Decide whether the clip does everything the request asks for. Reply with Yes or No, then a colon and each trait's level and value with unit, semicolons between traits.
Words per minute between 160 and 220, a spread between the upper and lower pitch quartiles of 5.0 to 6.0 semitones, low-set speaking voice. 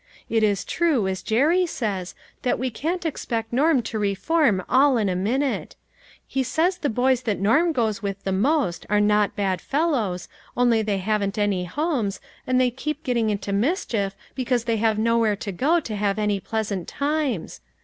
No: average, 180 wpm; average, 5.3 semitones; high, 225 Hz